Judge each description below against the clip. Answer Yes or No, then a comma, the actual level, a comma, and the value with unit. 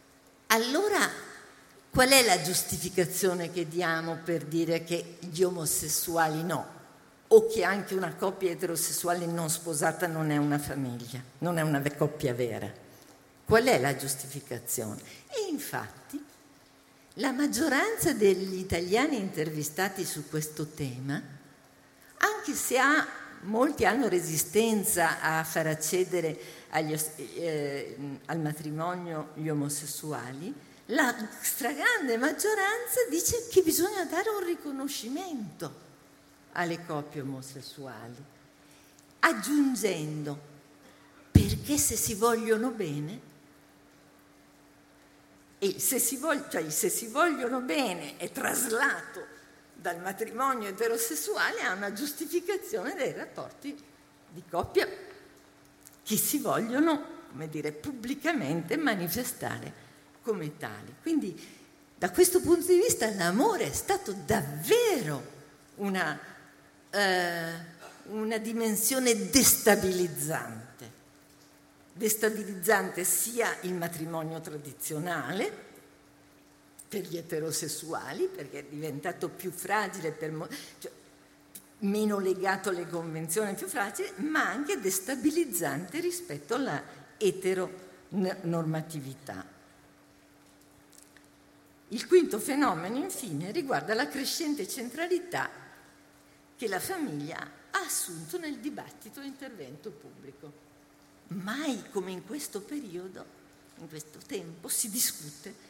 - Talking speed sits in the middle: No, slow, 100 wpm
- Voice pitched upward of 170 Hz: Yes, high, 190 Hz